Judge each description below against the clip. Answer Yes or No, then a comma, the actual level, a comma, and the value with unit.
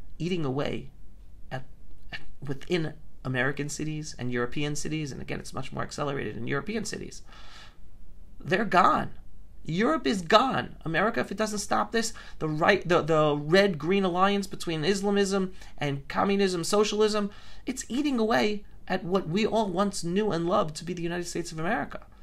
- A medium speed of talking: Yes, average, 160 wpm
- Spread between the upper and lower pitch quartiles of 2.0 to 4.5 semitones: No, average, 5.1 semitones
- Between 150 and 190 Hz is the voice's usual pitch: Yes, medium, 185 Hz